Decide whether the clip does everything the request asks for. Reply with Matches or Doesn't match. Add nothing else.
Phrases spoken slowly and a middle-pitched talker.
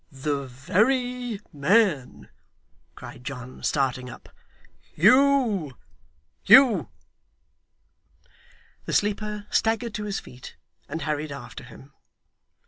Matches